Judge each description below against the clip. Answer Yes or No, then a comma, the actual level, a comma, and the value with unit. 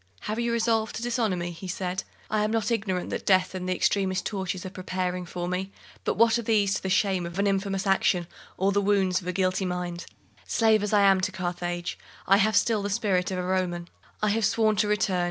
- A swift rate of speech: Yes, fast, 230 wpm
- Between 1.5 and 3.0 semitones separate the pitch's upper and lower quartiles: Yes, narrow, 2.5 semitones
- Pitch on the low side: No, high, 190 Hz